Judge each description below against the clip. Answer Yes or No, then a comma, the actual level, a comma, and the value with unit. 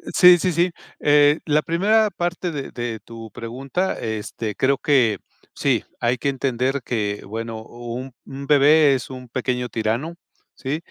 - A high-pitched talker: No, low, 135 Hz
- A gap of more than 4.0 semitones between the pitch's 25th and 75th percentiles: Yes, average, 4.5 semitones